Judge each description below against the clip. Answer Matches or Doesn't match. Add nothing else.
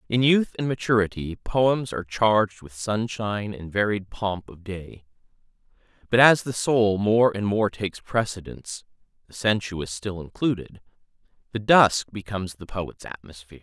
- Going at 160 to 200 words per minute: Doesn't match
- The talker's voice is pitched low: Matches